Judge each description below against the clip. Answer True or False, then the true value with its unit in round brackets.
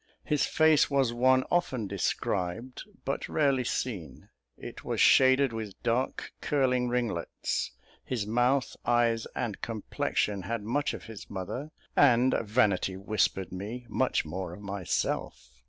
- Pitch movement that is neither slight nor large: True (4.5 semitones)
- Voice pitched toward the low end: True (115 Hz)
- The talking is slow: True (130 wpm)